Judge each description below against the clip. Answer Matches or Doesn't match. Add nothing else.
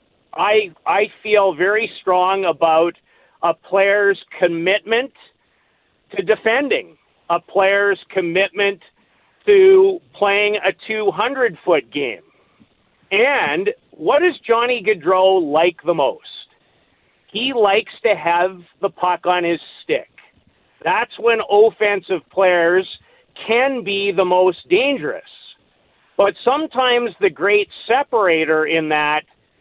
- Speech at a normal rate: Doesn't match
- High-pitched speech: Matches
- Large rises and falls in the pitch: Doesn't match